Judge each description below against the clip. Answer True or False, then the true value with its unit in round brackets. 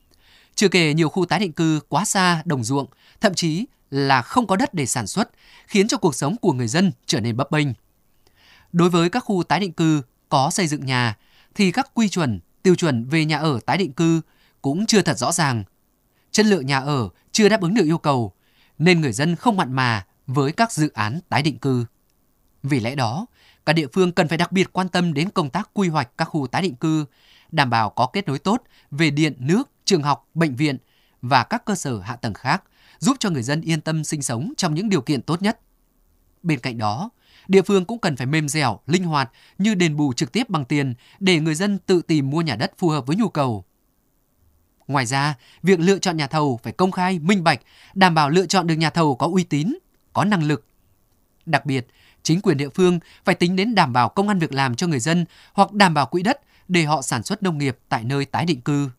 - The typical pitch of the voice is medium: True (160 Hz)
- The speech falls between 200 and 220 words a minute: False (235 wpm)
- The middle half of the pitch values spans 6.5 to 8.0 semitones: False (5.2 semitones)